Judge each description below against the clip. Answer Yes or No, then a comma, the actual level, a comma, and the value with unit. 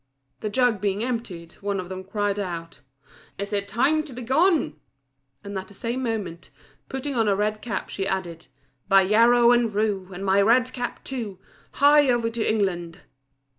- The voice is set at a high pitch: Yes, high, 210 Hz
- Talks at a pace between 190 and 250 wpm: No, average, 175 wpm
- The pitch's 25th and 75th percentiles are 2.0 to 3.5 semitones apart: No, average, 4.0 semitones